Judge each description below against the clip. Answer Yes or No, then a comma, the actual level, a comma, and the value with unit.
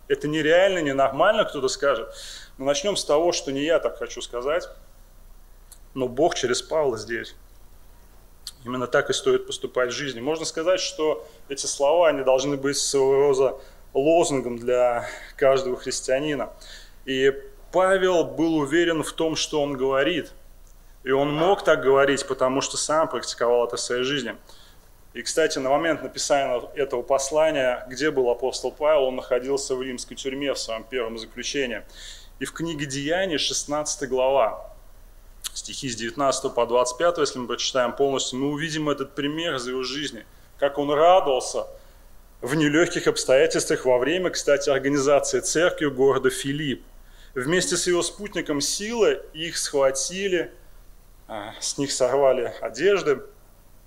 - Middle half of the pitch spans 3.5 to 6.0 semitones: Yes, average, 4.2 semitones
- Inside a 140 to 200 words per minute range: Yes, average, 145 wpm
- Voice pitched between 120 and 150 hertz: Yes, medium, 140 Hz